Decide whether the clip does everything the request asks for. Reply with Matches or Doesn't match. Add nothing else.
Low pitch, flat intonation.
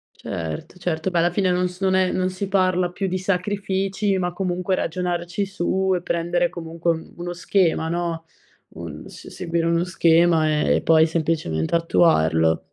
Doesn't match